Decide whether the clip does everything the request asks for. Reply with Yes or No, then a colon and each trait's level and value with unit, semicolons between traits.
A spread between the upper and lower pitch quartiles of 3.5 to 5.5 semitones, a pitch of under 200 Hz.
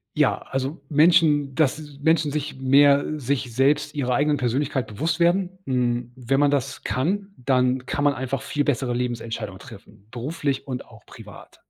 No: average, 3.0 semitones; low, 135 Hz